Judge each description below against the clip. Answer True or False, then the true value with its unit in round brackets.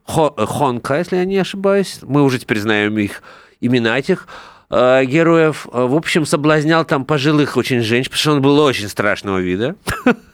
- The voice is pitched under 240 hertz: True (140 Hz)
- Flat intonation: False (5.2 semitones)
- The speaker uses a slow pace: False (155 wpm)